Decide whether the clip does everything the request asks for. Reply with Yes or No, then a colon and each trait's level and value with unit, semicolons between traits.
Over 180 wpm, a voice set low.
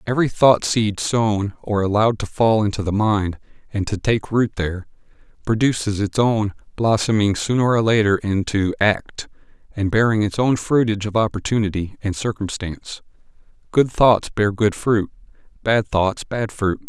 No: average, 155 wpm; low, 105 Hz